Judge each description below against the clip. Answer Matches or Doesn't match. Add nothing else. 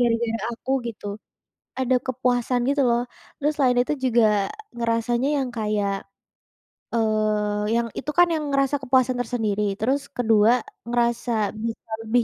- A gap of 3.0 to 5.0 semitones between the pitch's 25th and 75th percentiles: Doesn't match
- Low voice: Doesn't match